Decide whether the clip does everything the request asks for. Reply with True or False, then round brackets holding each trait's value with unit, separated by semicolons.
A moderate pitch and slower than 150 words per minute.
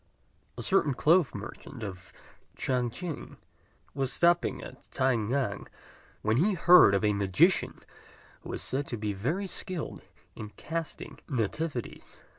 False (130 Hz; 135 wpm)